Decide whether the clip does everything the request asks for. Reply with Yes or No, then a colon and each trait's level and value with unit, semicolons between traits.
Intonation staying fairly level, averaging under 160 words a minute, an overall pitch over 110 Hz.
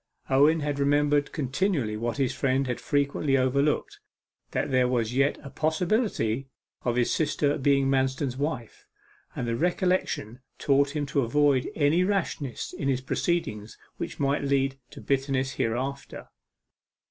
Yes: narrow, 2.3 semitones; average, 140 wpm; medium, 140 Hz